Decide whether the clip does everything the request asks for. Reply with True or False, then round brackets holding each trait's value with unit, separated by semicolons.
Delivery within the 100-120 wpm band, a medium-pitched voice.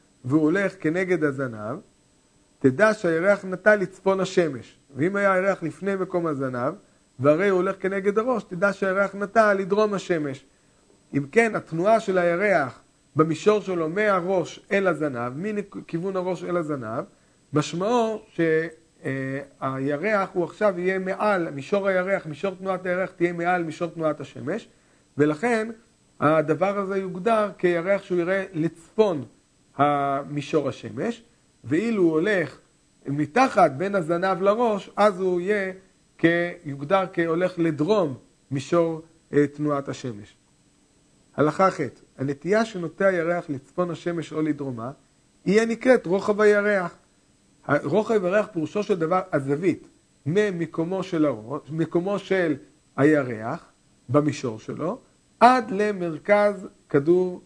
True (115 wpm; 175 Hz)